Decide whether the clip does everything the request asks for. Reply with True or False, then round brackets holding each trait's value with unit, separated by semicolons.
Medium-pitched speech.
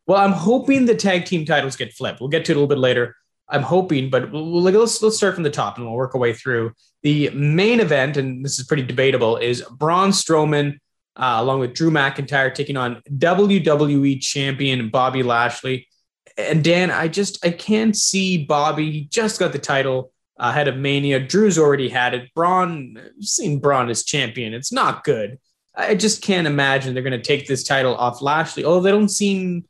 True (145 Hz)